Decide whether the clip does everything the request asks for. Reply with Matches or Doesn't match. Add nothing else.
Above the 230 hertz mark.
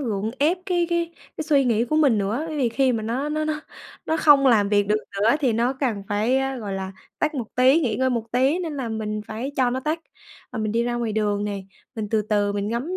Matches